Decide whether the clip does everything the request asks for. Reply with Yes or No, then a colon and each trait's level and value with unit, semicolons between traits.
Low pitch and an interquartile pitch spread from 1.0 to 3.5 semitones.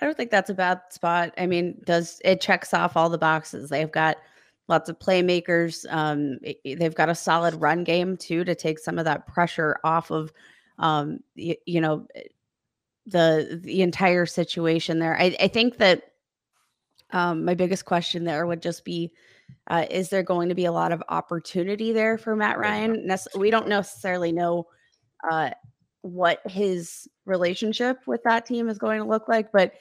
No: medium, 175 Hz; narrow, 2.6 semitones